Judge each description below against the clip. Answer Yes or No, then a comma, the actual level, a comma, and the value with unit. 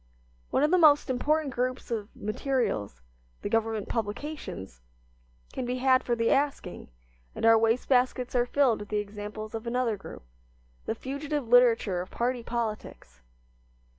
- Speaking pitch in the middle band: No, high, 240 Hz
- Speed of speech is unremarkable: Yes, average, 150 wpm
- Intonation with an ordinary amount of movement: Yes, average, 3.4 semitones